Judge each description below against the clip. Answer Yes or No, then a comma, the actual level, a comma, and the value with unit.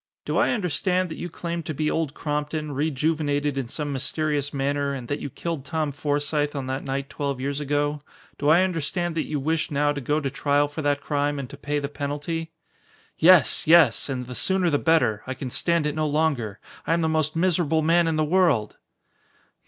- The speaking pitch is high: No, medium, 150 Hz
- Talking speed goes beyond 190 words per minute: Yes, fast, 205 wpm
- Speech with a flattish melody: Yes, narrow, 2.3 semitones